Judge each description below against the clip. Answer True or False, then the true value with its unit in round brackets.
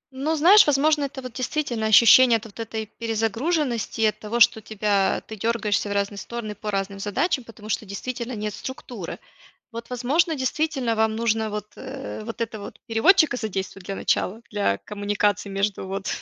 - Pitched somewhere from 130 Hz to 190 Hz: False (225 Hz)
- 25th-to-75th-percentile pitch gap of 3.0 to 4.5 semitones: True (3.7 semitones)